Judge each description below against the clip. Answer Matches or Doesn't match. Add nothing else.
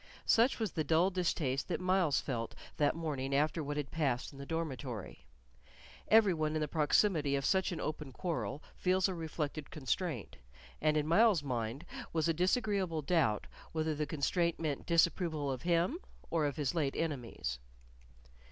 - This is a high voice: Doesn't match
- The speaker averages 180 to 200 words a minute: Doesn't match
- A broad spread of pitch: Doesn't match